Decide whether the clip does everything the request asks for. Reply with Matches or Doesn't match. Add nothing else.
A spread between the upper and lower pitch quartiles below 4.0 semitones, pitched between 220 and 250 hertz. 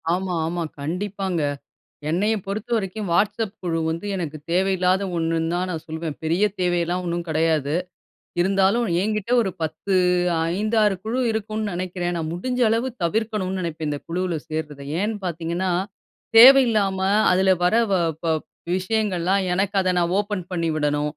Doesn't match